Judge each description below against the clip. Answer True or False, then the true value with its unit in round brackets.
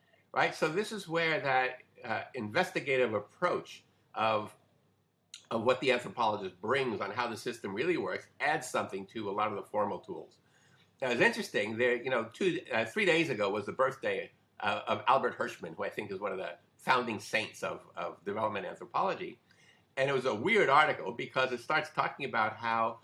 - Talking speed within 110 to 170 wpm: False (190 wpm)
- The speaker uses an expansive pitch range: True (6.9 semitones)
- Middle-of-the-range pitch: False (130 Hz)